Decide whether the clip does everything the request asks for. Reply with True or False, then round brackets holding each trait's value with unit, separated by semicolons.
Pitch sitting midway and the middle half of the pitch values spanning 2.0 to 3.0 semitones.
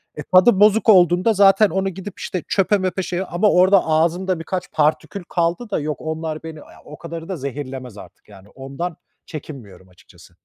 False (170 Hz; 4.1 semitones)